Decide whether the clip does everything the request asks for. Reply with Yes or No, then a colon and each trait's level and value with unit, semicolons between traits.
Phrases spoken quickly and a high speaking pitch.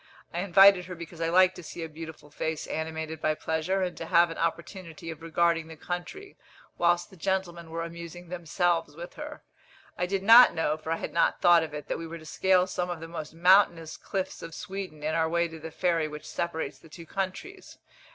No: fast, 220 wpm; medium, 170 Hz